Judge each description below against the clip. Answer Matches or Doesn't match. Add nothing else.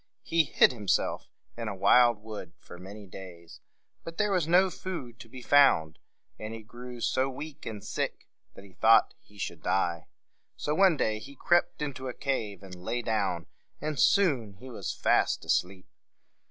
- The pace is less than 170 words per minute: Doesn't match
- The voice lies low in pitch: Matches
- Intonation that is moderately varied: Doesn't match